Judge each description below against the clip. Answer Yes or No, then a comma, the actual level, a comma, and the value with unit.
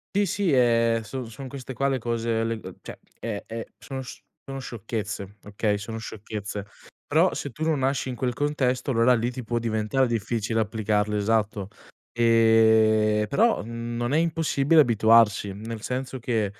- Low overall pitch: Yes, low, 115 Hz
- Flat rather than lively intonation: No, average, 3.2 semitones